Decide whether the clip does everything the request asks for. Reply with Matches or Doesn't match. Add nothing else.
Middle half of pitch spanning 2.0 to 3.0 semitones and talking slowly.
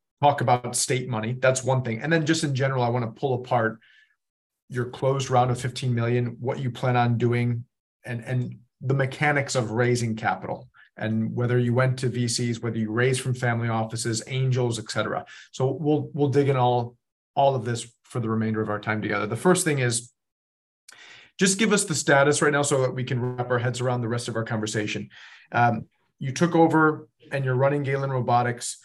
Doesn't match